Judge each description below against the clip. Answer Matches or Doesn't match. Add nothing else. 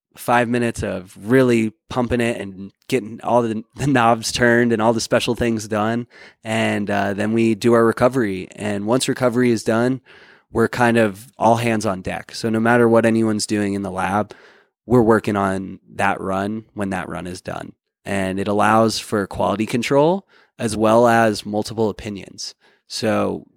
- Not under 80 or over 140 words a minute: Doesn't match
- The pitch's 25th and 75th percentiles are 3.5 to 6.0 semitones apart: Doesn't match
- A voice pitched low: Matches